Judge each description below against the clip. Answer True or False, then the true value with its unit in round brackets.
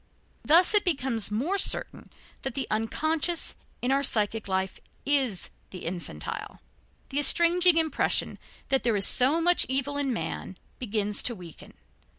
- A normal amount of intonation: False (7.1 semitones)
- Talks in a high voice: True (260 Hz)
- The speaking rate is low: False (145 wpm)